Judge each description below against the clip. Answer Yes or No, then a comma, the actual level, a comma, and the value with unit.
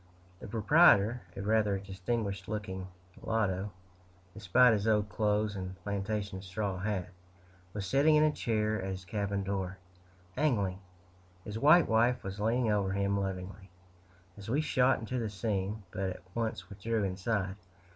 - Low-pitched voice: Yes, low, 105 Hz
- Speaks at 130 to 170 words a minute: Yes, average, 145 wpm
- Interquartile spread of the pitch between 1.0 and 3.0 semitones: Yes, narrow, 2.6 semitones